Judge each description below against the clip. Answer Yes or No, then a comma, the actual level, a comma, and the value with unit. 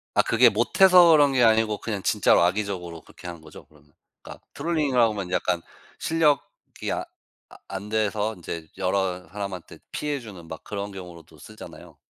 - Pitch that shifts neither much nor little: Yes, average, 4.8 semitones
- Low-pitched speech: Yes, low, 100 Hz